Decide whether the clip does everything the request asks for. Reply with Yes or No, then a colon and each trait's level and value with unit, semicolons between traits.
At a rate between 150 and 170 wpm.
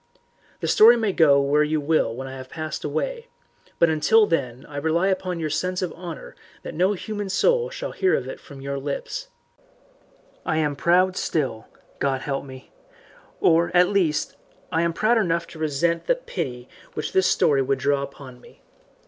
No: average, 180 wpm